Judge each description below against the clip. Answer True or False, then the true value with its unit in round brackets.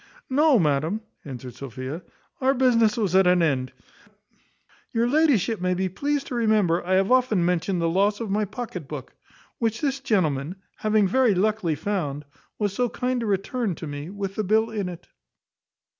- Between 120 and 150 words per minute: False (175 wpm)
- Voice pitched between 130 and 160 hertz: False (200 Hz)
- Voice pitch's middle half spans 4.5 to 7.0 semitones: True (5.2 semitones)